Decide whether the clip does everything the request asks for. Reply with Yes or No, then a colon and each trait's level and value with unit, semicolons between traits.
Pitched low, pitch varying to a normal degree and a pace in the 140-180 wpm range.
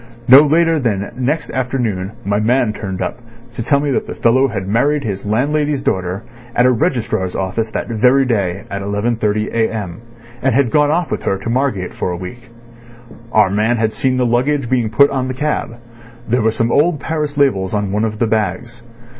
No: low, 115 Hz; average, 4.6 semitones; average, 195 wpm